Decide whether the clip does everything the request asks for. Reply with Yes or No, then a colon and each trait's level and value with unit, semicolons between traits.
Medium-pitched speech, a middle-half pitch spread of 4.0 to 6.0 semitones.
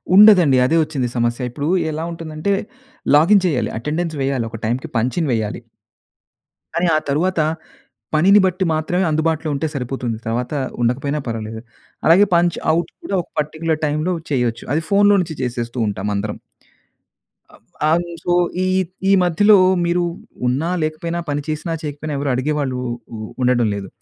Yes: medium, 150 Hz; average, 5.2 semitones